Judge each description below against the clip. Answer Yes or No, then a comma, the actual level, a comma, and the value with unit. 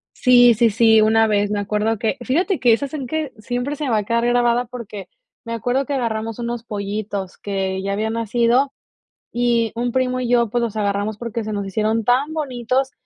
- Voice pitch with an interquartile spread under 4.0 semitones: Yes, narrow, 2.5 semitones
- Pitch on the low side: No, high, 230 Hz